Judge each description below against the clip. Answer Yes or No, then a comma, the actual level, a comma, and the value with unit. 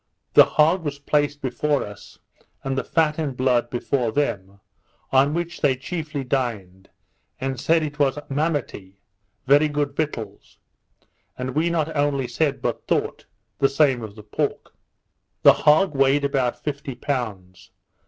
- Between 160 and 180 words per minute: No, average, 145 wpm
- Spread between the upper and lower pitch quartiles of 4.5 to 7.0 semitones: No, average, 3.4 semitones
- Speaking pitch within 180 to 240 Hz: No, medium, 140 Hz